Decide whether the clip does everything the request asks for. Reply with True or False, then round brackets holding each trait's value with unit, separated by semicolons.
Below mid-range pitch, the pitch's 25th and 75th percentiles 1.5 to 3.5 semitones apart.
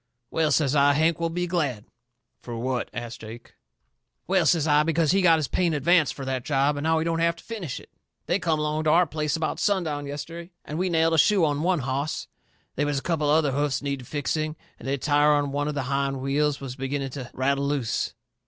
False (150 Hz; 2.9 semitones)